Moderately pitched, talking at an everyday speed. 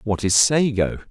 No: low, 110 Hz; average, 165 wpm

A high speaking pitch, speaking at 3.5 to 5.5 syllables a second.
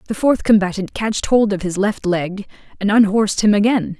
Yes: high, 205 Hz; 4.9 syllables/s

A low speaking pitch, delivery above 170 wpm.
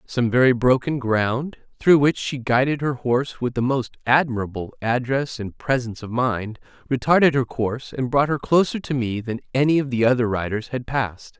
Yes: low, 125 Hz; average, 190 wpm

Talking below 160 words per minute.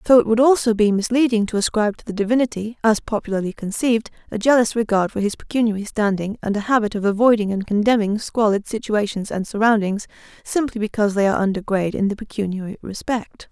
No: average, 185 wpm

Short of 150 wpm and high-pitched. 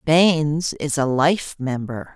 No: average, 140 wpm; medium, 150 Hz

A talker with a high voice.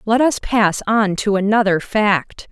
Yes: high, 210 Hz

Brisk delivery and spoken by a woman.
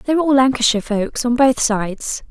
Yes: fast, 210 wpm; female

